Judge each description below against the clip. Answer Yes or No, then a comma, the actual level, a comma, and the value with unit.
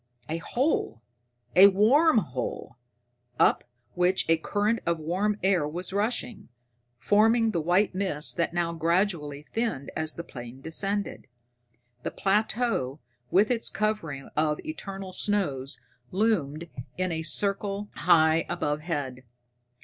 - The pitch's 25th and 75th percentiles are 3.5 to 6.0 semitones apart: Yes, average, 5.0 semitones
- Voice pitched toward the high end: No, medium, 180 Hz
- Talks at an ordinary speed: No, slow, 125 wpm